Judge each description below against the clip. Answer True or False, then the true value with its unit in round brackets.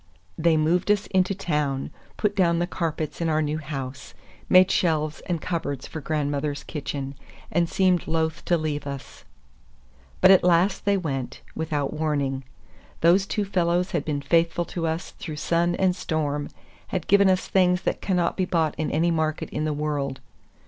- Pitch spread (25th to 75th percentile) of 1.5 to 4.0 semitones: True (3.2 semitones)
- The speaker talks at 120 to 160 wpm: False (170 wpm)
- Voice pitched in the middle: True (160 Hz)